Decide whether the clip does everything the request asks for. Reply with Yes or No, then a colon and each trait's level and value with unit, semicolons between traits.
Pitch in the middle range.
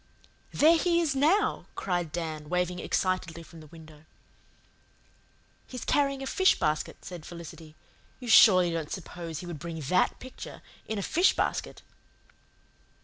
Yes: medium, 175 Hz